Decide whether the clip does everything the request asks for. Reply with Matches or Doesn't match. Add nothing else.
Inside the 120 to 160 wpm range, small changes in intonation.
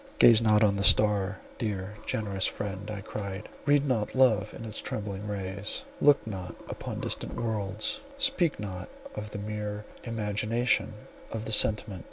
Matches